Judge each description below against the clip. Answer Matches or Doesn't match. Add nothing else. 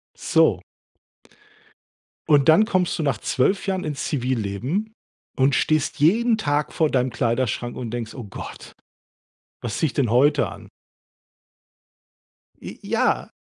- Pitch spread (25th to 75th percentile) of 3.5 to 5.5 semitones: Matches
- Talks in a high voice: Doesn't match